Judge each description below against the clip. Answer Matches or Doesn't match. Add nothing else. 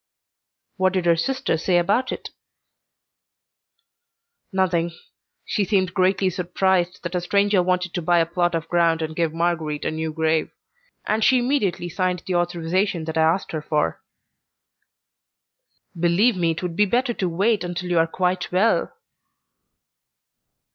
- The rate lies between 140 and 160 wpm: Matches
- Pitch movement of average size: Doesn't match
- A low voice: Doesn't match